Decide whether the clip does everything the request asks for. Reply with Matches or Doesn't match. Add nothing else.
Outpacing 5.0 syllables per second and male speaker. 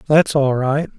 Doesn't match